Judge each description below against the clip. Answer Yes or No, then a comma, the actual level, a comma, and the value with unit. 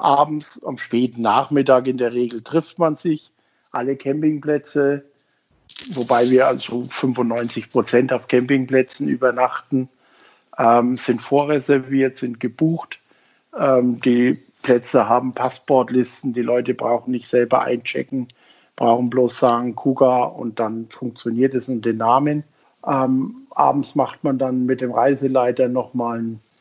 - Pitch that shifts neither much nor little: No, narrow, 2.1 semitones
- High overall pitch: No, low, 130 Hz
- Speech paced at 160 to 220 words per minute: No, average, 130 wpm